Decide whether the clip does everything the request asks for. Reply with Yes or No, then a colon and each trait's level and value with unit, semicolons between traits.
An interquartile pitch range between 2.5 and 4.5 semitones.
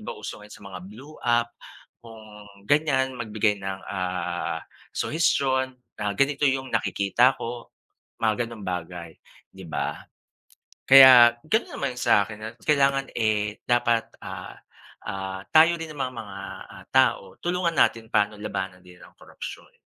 No: average, 5.0 semitones